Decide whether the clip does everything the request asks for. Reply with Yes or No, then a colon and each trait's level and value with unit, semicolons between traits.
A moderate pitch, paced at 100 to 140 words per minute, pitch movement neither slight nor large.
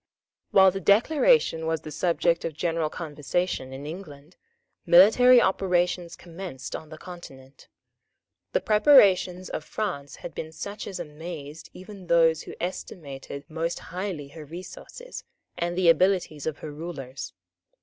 Yes: medium, 170 Hz; slow, 135 wpm; average, 3.4 semitones